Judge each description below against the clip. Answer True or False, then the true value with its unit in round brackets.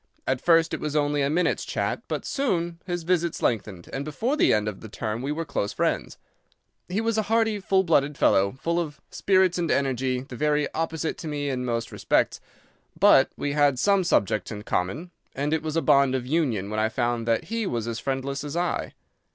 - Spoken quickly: True (210 wpm)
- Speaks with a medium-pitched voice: True (145 Hz)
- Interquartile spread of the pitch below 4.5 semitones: False (5.5 semitones)